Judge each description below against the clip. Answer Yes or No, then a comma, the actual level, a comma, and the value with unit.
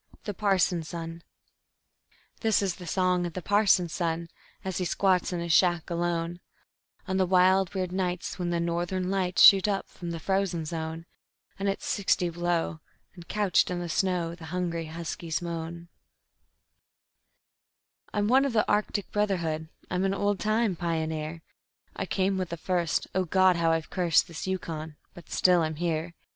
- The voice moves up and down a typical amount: No, narrow, 2.2 semitones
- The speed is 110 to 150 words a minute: No, average, 165 wpm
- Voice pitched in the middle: Yes, medium, 175 Hz